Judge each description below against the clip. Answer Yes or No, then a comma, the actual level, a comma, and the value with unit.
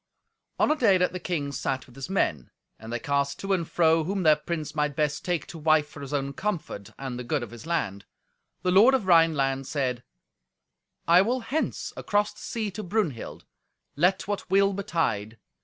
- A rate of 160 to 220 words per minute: Yes, average, 195 wpm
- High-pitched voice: No, medium, 160 Hz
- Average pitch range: No, wide, 5.9 semitones